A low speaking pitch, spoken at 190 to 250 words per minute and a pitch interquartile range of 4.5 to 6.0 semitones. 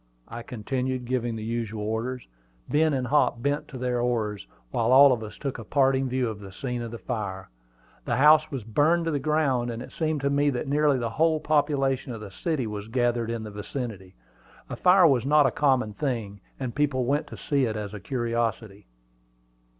No: low, 125 Hz; fast, 205 wpm; average, 4.0 semitones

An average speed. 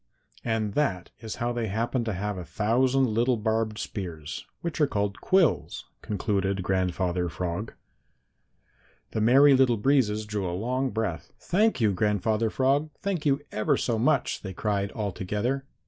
Yes: average, 155 wpm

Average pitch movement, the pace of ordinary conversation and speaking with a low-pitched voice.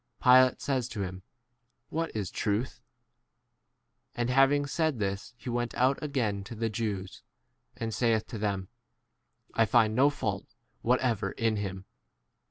Yes: average, 3.9 semitones; average, 150 wpm; low, 115 Hz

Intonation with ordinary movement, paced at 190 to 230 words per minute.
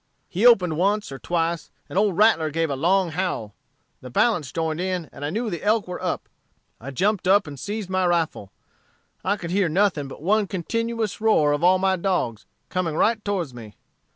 Yes: average, 4.4 semitones; average, 195 wpm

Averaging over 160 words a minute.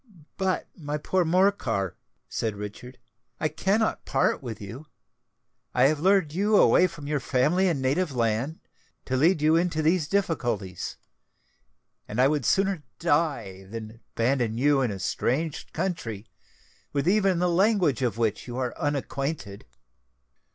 No: average, 145 wpm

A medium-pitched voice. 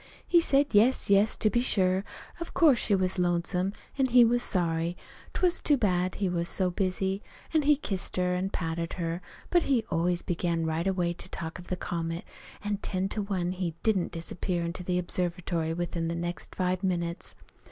Yes: medium, 180 Hz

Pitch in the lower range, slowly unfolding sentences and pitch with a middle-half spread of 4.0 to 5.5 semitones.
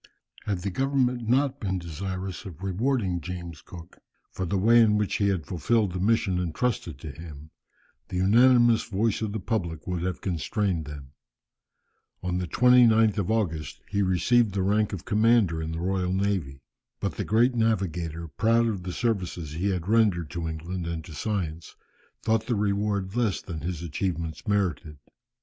No: very low, 95 Hz; average, 170 wpm; average, 4.6 semitones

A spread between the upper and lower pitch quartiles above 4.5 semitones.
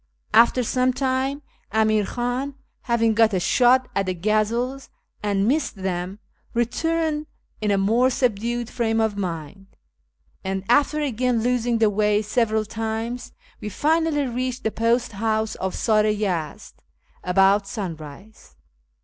No: average, 3.5 semitones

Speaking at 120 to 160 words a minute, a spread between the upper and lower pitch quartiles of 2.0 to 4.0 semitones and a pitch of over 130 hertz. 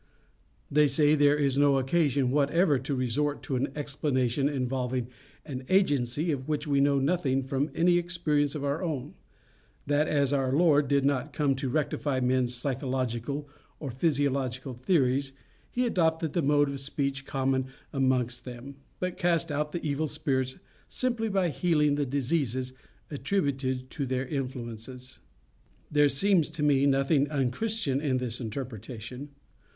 Yes: average, 145 wpm; narrow, 2.5 semitones; medium, 140 Hz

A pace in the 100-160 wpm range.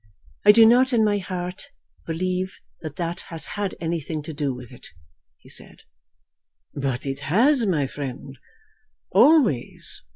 Yes: average, 140 wpm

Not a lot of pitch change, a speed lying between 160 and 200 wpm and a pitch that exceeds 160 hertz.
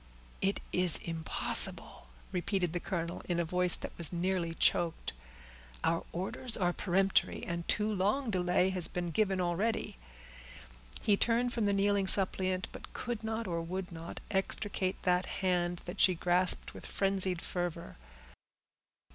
No: narrow, 2.3 semitones; average, 145 wpm; medium, 185 Hz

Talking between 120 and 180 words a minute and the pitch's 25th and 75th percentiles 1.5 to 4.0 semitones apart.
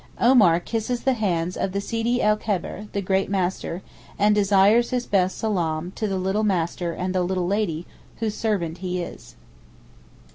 Yes: average, 170 wpm; average, 3.0 semitones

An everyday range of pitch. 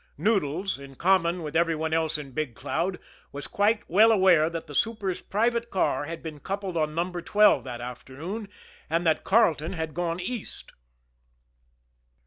Yes: average, 4.1 semitones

